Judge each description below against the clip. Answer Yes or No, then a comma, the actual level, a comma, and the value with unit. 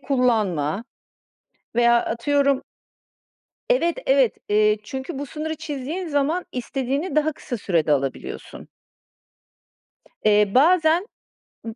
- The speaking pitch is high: Yes, very high, 265 Hz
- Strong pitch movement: Yes, wide, 6.1 semitones